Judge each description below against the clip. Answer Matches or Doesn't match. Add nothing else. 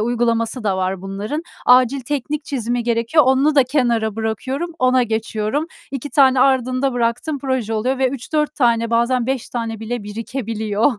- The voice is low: Doesn't match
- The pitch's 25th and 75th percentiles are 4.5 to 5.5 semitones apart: Doesn't match